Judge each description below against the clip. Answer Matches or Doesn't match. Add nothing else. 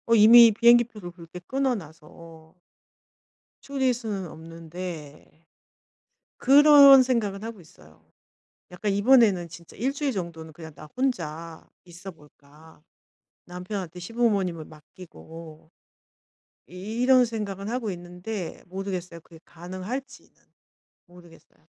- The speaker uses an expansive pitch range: Matches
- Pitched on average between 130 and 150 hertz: Doesn't match